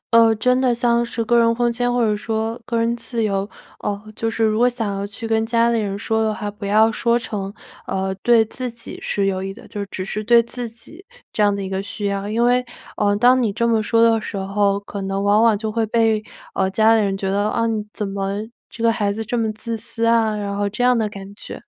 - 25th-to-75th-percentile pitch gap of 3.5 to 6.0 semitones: No, narrow, 2.4 semitones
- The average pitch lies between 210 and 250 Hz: Yes, high, 220 Hz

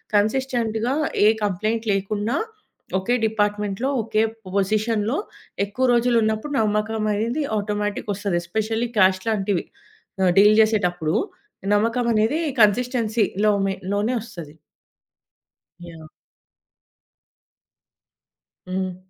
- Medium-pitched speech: No, high, 215 Hz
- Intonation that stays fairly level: Yes, narrow, 2.3 semitones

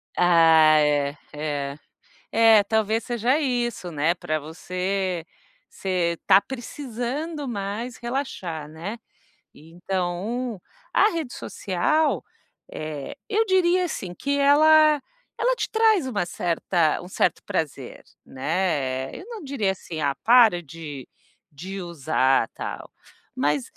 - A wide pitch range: Yes, wide, 8.0 semitones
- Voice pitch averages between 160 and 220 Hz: Yes, high, 190 Hz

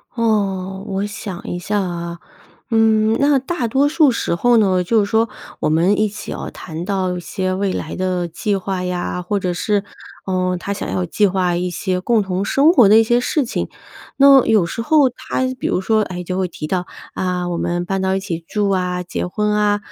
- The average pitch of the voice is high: Yes, high, 195 Hz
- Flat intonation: No, average, 3.4 semitones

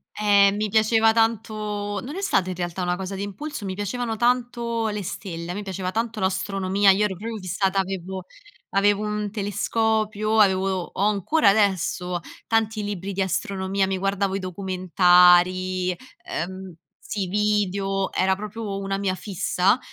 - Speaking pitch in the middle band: No, high, 195 Hz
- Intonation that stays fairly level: Yes, narrow, 2.2 semitones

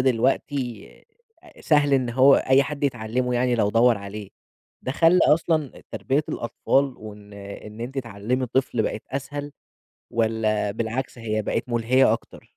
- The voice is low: Yes, low, 125 Hz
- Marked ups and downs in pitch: No, average, 3.6 semitones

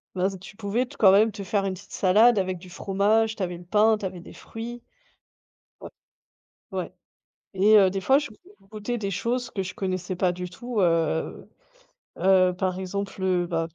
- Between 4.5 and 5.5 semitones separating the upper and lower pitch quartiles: No, average, 2.8 semitones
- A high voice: Yes, high, 195 Hz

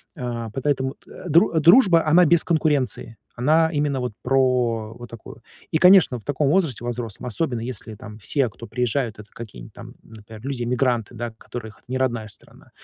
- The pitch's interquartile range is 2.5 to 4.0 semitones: No, average, 4.4 semitones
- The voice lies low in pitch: Yes, low, 125 Hz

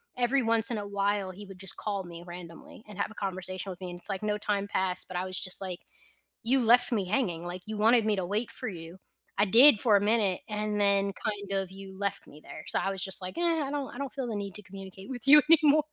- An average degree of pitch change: Yes, average, 3.2 semitones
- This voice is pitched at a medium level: No, high, 200 Hz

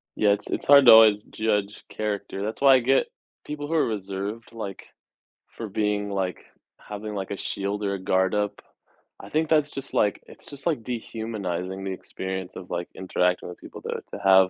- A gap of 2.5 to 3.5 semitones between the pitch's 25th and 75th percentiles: Yes, average, 3.0 semitones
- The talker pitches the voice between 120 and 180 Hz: No, low, 105 Hz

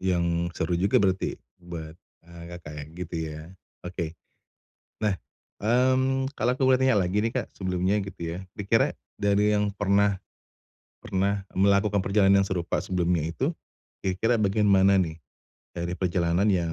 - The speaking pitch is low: Yes, very low, 95 Hz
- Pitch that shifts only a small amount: No, average, 3.0 semitones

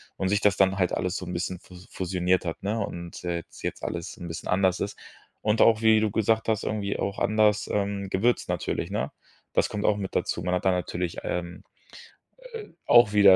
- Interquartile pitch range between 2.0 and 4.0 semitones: Yes, average, 2.8 semitones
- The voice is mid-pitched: No, low, 100 Hz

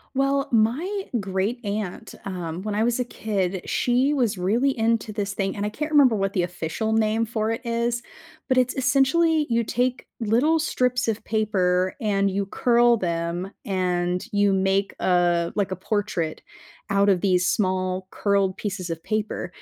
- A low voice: No, high, 210 Hz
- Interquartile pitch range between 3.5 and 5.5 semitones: Yes, average, 4.2 semitones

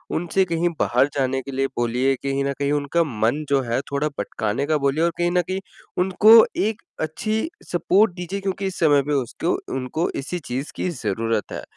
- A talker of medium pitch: Yes, medium, 145 Hz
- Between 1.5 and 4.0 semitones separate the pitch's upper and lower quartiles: No, average, 4.8 semitones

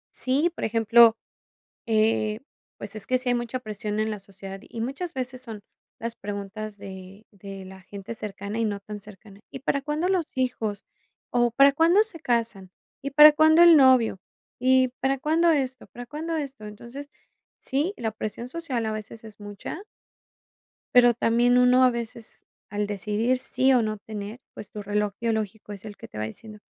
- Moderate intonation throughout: Yes, average, 3.8 semitones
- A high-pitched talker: Yes, high, 230 Hz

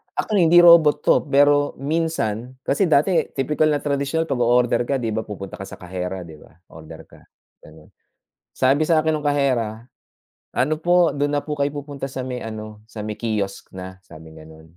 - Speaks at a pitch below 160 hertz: Yes, low, 135 Hz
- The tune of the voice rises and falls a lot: Yes, wide, 5.9 semitones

